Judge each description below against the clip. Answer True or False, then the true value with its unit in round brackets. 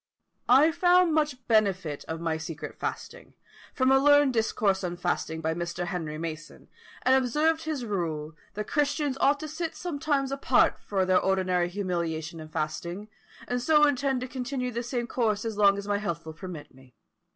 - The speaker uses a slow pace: False (175 wpm)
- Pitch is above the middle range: True (210 Hz)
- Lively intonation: True (8.0 semitones)